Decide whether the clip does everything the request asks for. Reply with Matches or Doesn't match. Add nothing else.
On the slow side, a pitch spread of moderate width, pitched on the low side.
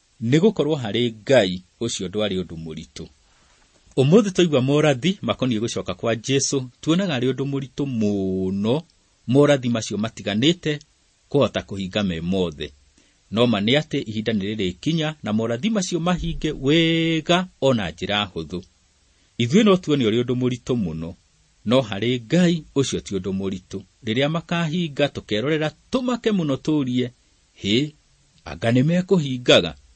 Doesn't match